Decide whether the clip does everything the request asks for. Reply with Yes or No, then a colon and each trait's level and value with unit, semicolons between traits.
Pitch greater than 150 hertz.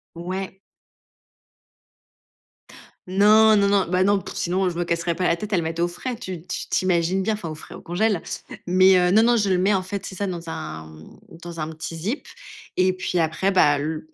Yes: medium, 185 Hz